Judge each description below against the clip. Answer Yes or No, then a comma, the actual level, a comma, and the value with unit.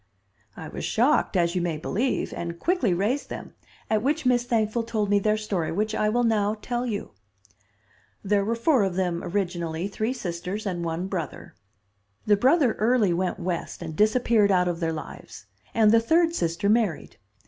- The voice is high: Yes, high, 205 Hz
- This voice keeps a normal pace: Yes, average, 180 wpm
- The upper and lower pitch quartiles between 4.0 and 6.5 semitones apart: Yes, average, 4.7 semitones